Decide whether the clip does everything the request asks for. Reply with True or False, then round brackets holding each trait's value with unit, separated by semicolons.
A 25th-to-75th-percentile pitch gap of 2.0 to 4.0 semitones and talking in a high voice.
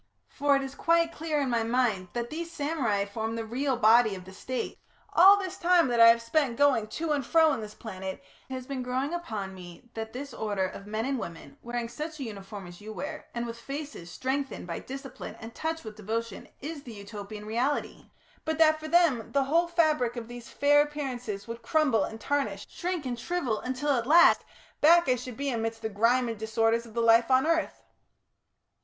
False (4.8 semitones; 245 Hz)